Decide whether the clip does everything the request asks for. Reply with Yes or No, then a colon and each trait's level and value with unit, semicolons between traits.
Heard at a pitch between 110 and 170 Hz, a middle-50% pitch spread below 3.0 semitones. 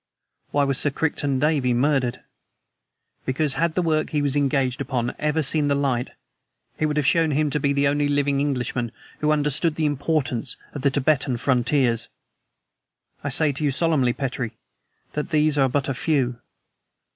Yes: medium, 140 Hz; narrow, 2.5 semitones